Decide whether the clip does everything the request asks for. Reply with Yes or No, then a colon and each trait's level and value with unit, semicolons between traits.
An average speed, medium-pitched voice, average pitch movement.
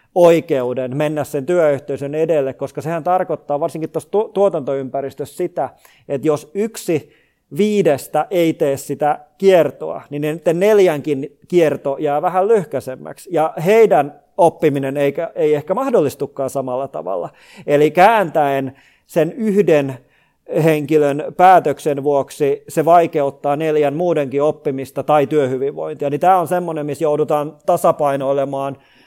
Yes: average, 115 wpm; medium, 150 Hz; average, 3.1 semitones